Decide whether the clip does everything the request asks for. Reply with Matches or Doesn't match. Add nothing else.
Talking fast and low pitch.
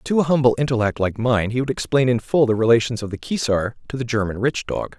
Matches